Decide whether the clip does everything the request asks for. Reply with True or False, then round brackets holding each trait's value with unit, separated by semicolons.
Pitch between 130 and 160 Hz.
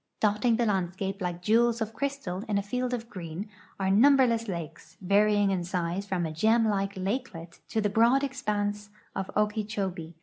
False (205 Hz)